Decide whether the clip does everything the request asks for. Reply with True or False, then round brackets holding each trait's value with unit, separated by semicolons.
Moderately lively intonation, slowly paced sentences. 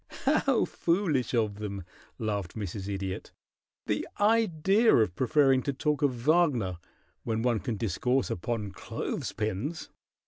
False (6.7 semitones; 130 wpm)